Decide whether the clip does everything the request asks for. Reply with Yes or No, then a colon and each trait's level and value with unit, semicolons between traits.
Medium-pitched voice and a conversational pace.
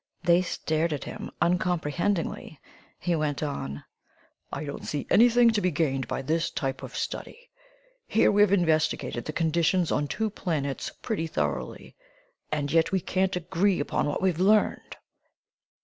Yes: medium, 165 Hz; average, 150 wpm